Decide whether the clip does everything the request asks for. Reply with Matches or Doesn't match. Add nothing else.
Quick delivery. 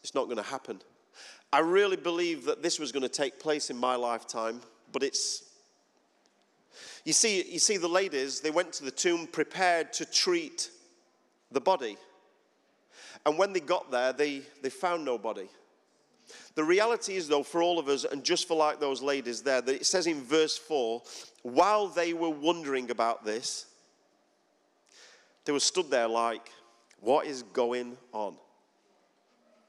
Doesn't match